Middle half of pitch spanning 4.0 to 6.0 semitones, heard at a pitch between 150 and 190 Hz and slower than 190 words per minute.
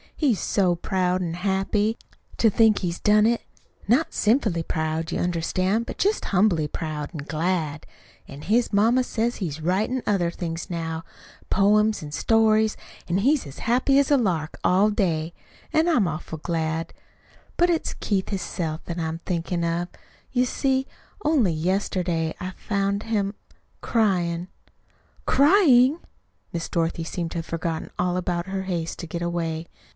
Yes: average, 4.8 semitones; medium, 185 Hz; average, 150 wpm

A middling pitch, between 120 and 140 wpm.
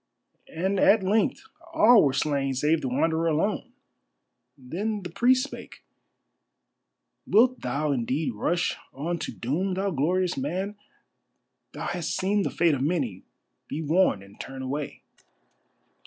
Yes: medium, 165 Hz; slow, 135 wpm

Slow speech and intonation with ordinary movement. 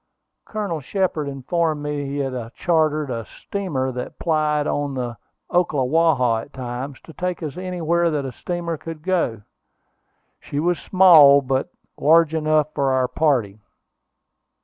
No: average, 145 wpm; average, 4.1 semitones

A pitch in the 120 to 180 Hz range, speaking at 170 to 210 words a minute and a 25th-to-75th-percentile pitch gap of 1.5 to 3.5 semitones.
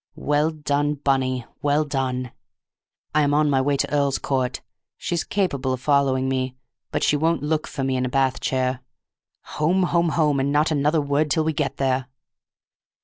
Yes: medium, 140 Hz; average, 175 wpm; narrow, 2.4 semitones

